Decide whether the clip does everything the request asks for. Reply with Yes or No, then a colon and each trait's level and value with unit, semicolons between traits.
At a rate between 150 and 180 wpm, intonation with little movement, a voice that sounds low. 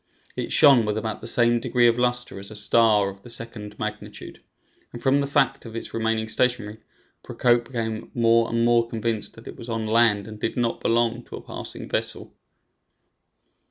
No: average, 190 wpm; narrow, 1.5 semitones; low, 115 Hz